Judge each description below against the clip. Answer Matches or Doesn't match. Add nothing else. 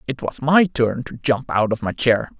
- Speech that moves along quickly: Matches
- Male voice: Matches